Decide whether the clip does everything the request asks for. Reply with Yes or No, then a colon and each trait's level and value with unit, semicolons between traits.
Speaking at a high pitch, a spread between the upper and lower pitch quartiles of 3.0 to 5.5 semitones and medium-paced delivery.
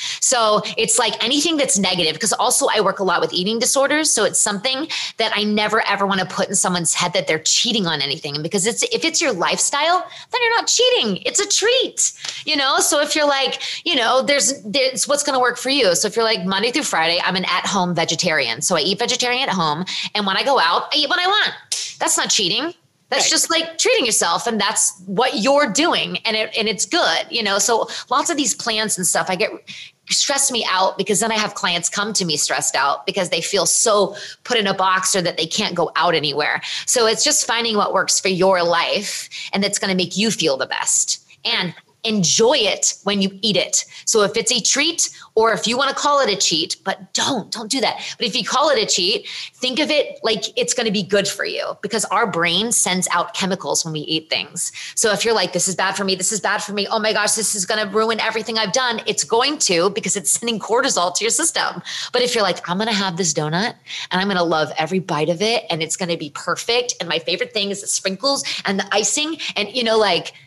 No: high, 215 Hz; average, 5.1 semitones; fast, 250 wpm